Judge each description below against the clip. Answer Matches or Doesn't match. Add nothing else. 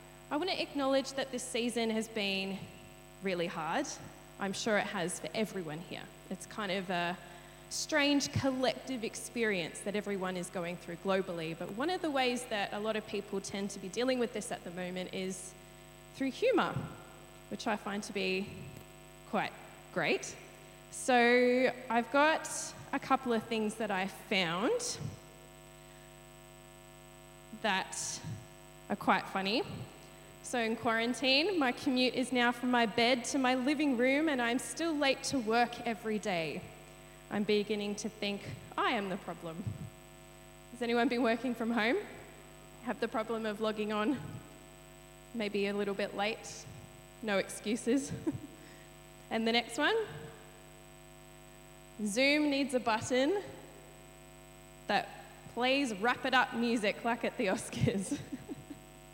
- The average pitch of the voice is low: Doesn't match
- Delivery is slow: Doesn't match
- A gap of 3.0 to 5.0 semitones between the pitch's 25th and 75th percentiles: Matches